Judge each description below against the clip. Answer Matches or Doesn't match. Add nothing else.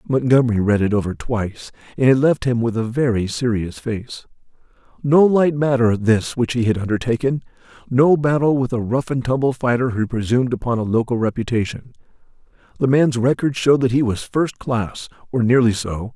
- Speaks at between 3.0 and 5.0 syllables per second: Doesn't match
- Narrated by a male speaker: Matches